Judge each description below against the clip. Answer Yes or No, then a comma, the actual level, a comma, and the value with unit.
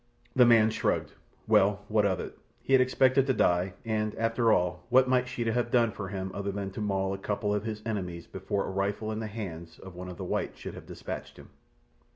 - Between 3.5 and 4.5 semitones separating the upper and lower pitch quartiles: No, average, 3.1 semitones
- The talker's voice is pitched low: Yes, low, 105 Hz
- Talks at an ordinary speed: No, fast, 225 wpm